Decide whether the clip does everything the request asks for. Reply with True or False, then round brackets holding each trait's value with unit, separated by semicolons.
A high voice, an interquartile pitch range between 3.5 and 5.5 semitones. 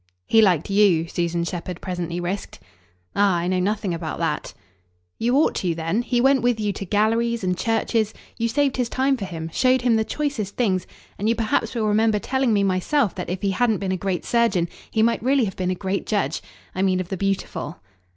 True (205 Hz; 4.2 semitones)